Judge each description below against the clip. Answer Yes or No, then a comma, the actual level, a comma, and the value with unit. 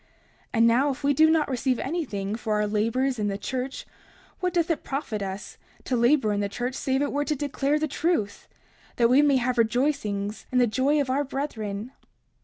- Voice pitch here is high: Yes, very high, 255 Hz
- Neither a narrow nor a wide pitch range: Yes, average, 4.9 semitones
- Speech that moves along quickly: Yes, fast, 210 wpm